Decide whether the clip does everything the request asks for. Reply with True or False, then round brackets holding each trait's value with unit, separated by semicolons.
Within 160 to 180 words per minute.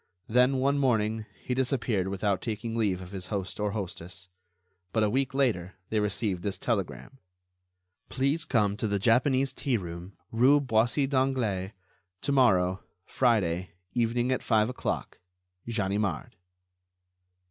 False (135 wpm)